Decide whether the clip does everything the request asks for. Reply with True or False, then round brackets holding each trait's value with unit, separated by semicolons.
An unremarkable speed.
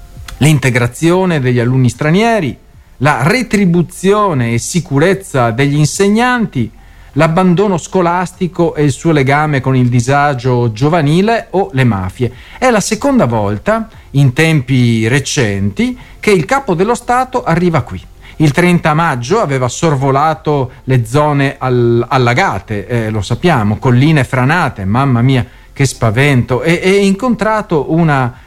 True (125 wpm)